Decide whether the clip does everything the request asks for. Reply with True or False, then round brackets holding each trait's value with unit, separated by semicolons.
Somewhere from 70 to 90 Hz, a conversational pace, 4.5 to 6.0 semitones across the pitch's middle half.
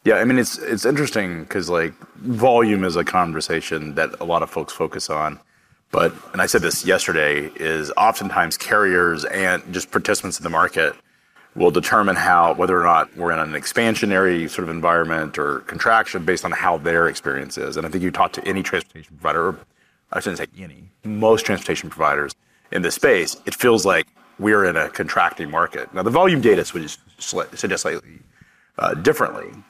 True (85 Hz; 185 wpm; 4.9 semitones)